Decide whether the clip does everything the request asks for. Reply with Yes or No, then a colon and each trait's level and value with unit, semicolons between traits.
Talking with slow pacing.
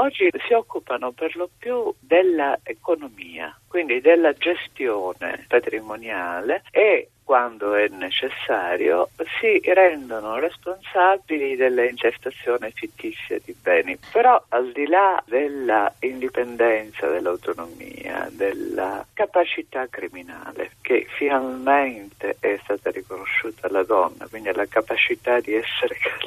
Yes: slow, 100 wpm